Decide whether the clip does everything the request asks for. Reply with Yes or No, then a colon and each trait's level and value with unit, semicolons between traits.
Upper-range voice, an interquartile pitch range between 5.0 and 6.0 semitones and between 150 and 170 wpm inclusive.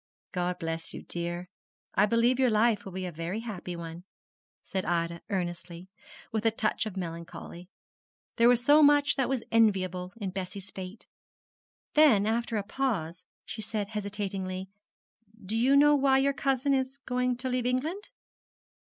Yes: high, 210 Hz; wide, 5.6 semitones; average, 165 wpm